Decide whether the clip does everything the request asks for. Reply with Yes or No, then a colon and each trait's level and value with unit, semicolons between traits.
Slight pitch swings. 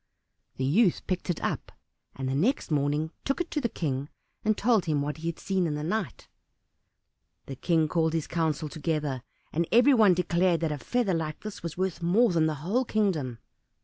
No: average, 4.6 semitones